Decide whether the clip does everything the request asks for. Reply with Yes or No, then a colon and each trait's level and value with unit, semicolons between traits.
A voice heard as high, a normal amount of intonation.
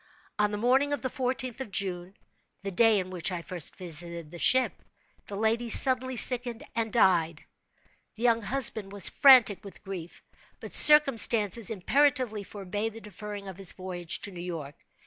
Yes: high, 210 Hz; average, 4.8 semitones